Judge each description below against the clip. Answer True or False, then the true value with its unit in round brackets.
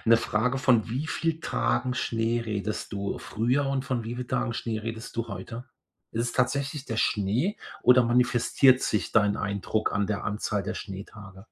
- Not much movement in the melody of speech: False (3.2 semitones)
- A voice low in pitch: True (115 Hz)